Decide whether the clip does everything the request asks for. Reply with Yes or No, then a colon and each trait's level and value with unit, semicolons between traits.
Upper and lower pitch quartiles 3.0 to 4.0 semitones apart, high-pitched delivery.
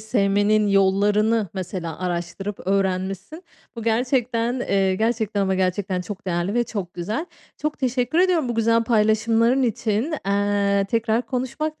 Yes: average, 3.5 semitones; high, 215 Hz